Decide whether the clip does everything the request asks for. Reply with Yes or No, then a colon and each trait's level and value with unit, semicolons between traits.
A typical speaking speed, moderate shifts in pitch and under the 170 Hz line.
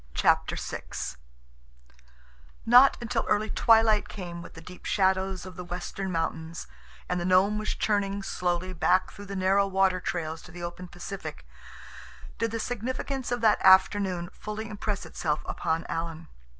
No: average, 150 wpm; average, 3.1 semitones; high, 190 Hz